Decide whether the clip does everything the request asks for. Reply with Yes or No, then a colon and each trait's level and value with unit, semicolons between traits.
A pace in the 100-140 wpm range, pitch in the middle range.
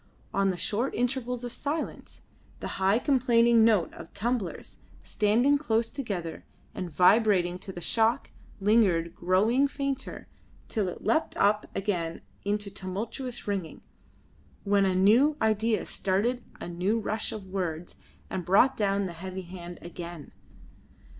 No: slow, 135 wpm; high, 205 Hz